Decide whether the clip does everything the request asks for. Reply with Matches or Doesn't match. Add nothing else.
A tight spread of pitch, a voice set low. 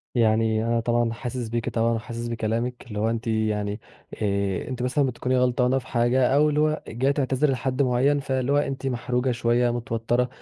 Matches